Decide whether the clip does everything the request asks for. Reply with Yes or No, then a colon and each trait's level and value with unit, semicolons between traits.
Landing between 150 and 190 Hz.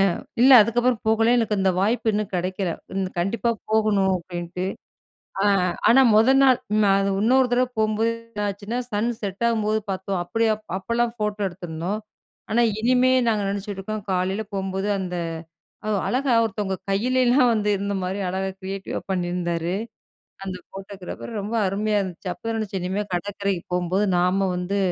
No: high, 200 Hz